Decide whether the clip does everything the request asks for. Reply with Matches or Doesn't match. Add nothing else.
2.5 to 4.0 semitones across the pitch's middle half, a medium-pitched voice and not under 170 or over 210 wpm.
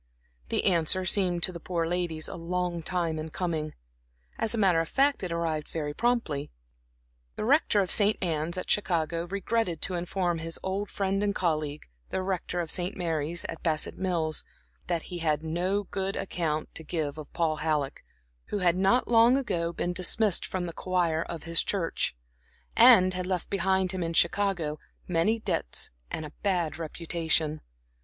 Matches